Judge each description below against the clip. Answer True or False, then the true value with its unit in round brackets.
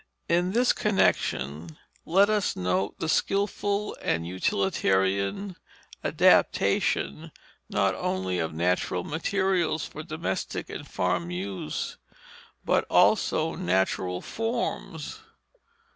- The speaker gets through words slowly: True (95 wpm)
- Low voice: True (95 Hz)